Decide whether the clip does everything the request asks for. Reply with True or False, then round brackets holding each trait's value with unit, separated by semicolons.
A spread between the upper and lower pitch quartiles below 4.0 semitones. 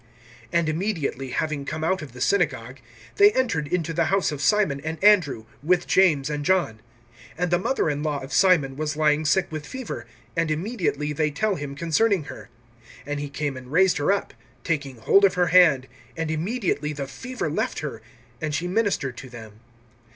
False (4.4 semitones)